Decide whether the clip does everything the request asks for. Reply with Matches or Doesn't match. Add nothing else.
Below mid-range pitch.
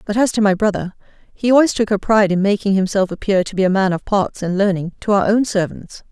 Doesn't match